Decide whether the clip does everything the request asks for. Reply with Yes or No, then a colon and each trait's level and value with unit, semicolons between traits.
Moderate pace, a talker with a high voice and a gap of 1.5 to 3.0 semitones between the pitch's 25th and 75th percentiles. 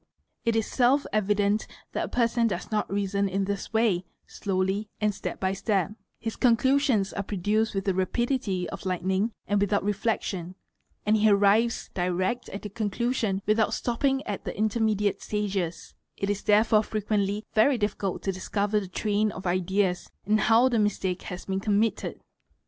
Yes: average, 165 wpm; high, 205 Hz; narrow, 2.4 semitones